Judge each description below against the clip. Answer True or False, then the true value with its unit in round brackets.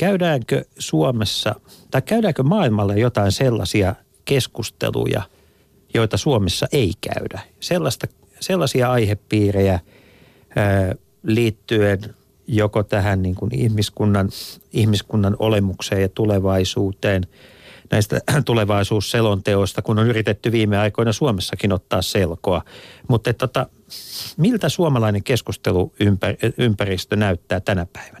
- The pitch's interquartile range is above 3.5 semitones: True (3.9 semitones)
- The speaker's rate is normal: False (90 wpm)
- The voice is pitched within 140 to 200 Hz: False (110 Hz)